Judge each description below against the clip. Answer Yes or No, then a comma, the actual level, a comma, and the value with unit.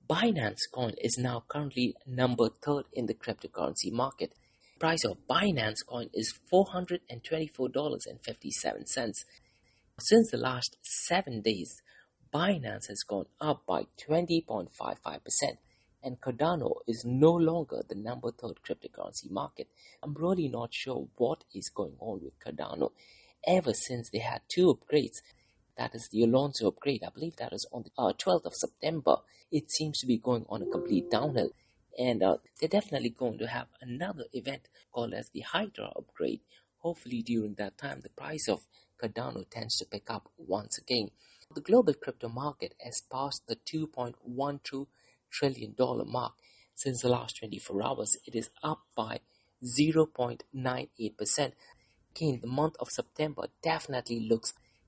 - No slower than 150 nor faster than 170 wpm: Yes, average, 155 wpm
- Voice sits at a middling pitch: No, low, 130 Hz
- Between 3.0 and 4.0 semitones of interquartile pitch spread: No, average, 4.5 semitones